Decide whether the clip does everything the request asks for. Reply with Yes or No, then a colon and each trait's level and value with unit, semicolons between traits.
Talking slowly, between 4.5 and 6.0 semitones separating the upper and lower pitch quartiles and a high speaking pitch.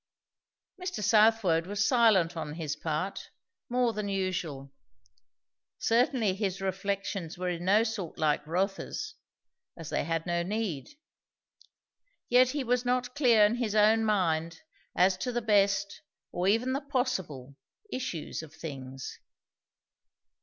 Yes: slow, 130 wpm; wide, 5.4 semitones; high, 195 Hz